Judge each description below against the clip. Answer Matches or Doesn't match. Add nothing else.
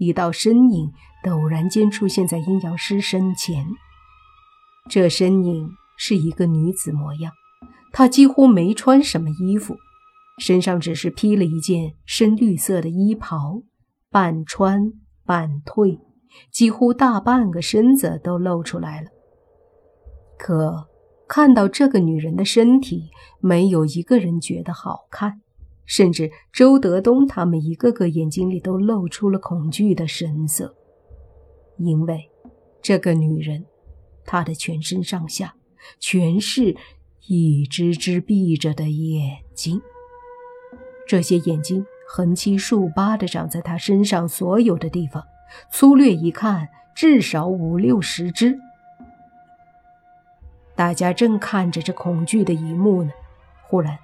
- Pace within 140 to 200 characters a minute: Matches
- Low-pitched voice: Doesn't match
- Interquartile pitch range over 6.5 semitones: Doesn't match